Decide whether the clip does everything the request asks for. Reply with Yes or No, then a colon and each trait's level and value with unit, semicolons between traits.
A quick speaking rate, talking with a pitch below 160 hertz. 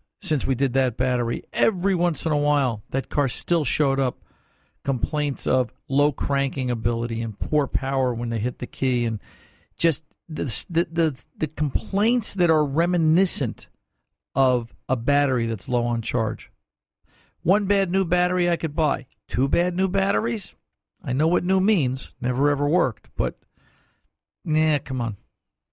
No: average, 160 wpm; low, 135 Hz